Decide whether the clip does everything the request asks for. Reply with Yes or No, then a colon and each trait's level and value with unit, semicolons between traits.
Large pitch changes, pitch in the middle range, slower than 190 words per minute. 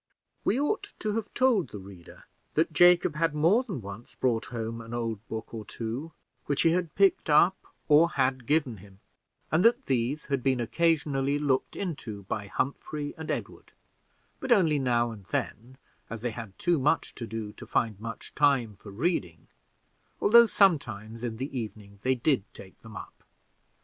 No: wide, 6.5 semitones; low, 130 Hz; average, 175 wpm